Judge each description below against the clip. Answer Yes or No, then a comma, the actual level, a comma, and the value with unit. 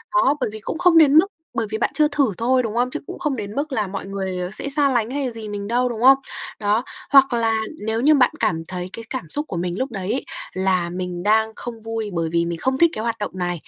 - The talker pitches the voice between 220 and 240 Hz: Yes, high, 225 Hz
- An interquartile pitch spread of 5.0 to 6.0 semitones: Yes, wide, 5.4 semitones